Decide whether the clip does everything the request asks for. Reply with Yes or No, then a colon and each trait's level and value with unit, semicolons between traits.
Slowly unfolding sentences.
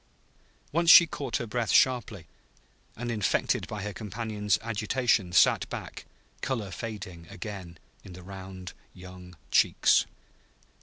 Yes: slow, 120 wpm